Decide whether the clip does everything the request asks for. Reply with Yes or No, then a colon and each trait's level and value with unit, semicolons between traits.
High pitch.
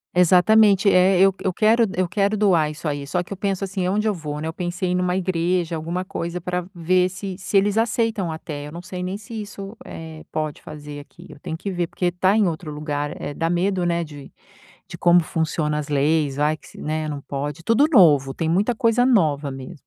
No: medium, 175 Hz